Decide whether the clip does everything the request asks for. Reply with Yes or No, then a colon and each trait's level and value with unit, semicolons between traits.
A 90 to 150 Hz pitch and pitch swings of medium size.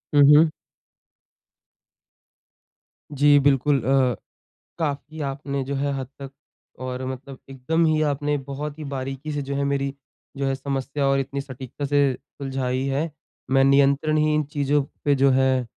No: medium, 140 Hz; narrow, 1.3 semitones